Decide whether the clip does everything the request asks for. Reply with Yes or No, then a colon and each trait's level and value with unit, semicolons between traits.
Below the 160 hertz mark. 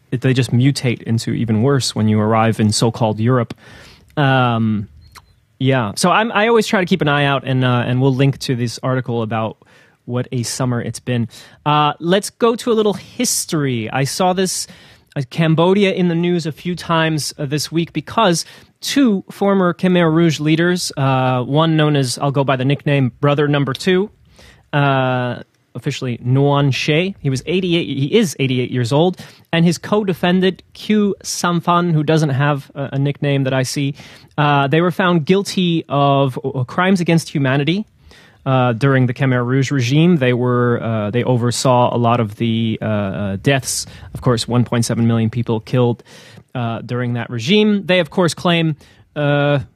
Yes: medium, 140 Hz